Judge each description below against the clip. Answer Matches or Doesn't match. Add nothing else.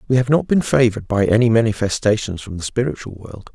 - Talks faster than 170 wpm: Matches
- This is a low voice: Matches